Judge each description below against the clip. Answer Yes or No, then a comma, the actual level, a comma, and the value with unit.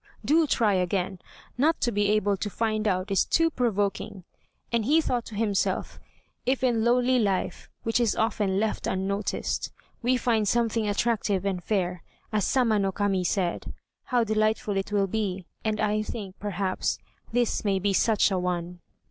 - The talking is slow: No, average, 165 wpm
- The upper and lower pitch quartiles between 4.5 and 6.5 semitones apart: No, average, 3.0 semitones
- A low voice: No, high, 210 Hz